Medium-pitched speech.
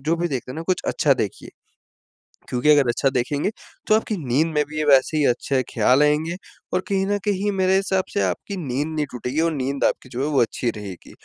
Yes: medium, 150 Hz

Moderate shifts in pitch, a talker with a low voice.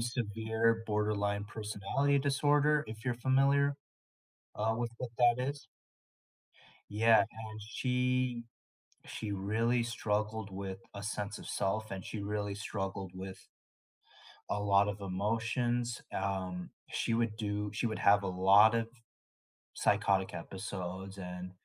Yes: average, 3.0 semitones; low, 105 Hz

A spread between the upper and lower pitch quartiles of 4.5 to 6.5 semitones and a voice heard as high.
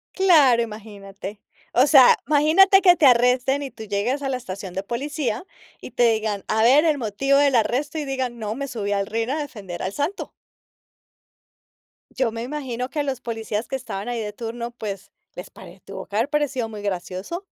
Yes: average, 4.9 semitones; high, 245 Hz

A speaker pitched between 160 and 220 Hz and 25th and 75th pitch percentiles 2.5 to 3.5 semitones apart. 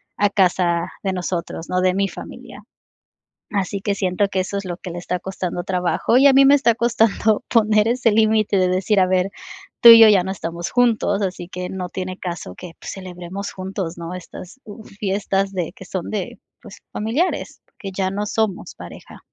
Yes: high, 190 Hz; average, 2.8 semitones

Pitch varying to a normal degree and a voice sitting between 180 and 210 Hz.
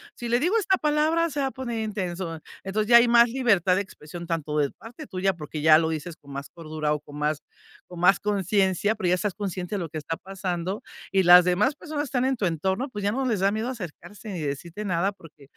No: wide, 5.7 semitones; high, 190 Hz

